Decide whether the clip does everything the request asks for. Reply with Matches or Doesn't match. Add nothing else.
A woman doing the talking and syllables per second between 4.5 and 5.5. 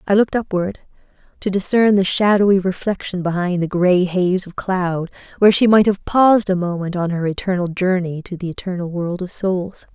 Matches